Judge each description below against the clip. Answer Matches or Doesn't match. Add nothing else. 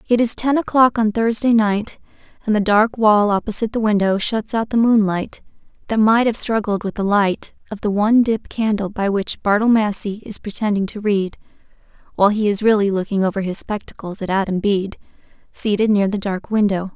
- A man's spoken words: Doesn't match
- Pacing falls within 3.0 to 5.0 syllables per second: Doesn't match